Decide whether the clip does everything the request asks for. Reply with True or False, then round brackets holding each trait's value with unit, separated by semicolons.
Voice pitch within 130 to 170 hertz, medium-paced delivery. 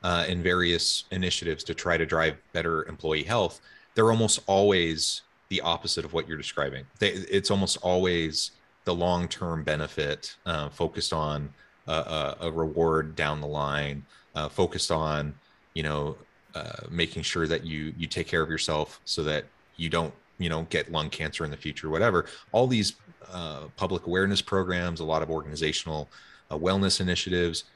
False (85 Hz; 165 wpm)